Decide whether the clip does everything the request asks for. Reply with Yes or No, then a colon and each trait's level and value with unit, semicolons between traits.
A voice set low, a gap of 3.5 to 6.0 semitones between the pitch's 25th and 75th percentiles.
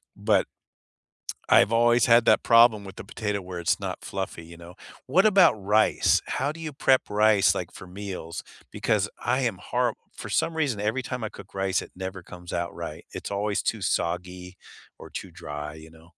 Yes: low, 100 Hz; average, 4.6 semitones